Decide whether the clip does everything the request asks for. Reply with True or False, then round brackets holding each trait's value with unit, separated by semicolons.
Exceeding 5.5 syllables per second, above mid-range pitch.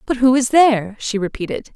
True (5.7 syllables/s; 240 Hz)